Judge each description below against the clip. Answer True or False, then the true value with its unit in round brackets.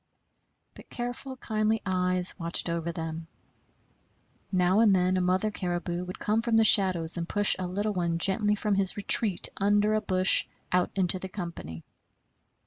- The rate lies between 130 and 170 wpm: True (160 wpm)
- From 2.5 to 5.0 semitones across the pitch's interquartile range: True (2.9 semitones)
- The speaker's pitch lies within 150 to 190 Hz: True (185 Hz)